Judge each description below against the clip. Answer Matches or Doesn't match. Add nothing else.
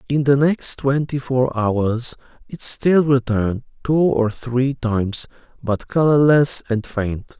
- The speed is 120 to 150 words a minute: Matches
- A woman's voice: Doesn't match